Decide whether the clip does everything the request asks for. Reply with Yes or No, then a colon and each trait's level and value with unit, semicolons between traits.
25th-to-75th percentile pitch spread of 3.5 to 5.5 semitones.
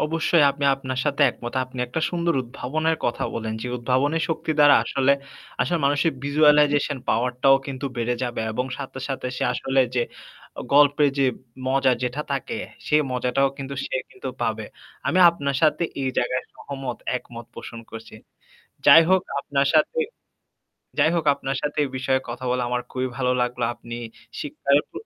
No: average, 2.8 semitones